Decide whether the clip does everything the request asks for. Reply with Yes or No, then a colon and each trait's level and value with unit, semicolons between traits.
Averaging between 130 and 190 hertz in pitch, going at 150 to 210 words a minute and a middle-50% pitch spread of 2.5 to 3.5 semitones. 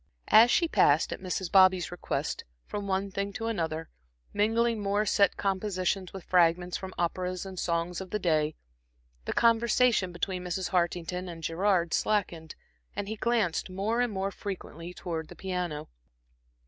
Yes: medium, 185 Hz; average, 155 wpm; average, 2.8 semitones